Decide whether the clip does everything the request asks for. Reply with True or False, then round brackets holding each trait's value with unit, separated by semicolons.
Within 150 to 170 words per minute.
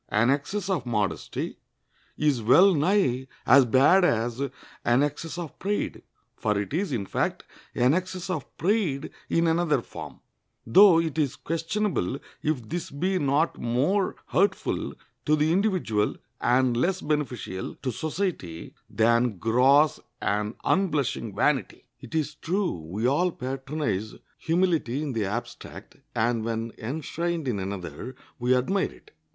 False (135 wpm)